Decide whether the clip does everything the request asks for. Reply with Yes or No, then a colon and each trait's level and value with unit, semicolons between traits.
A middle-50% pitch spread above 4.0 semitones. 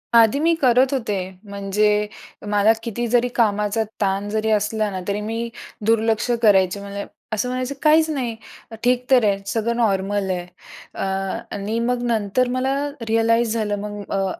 No: average, 2.8 semitones